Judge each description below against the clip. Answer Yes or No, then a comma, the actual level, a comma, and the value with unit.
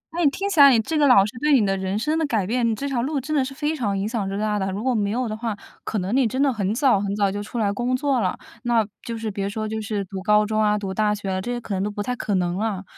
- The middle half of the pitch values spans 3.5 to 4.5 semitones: Yes, average, 4.0 semitones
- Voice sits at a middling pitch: No, high, 215 Hz